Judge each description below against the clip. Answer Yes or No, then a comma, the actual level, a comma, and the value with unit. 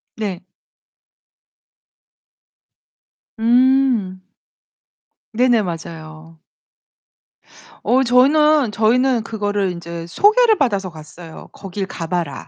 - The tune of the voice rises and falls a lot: Yes, wide, 6.7 semitones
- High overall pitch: Yes, high, 210 Hz